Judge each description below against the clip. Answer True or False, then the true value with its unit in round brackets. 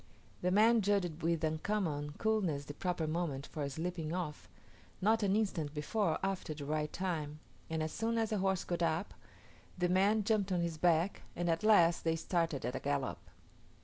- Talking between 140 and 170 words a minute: False (185 wpm)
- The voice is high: False (170 Hz)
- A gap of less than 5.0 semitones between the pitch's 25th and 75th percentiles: True (4.0 semitones)